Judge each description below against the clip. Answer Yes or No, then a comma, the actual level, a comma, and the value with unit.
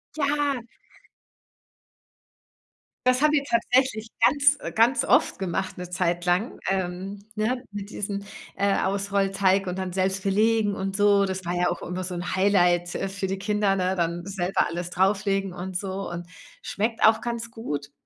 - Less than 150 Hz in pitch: No, high, 195 Hz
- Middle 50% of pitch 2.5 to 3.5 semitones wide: Yes, average, 2.9 semitones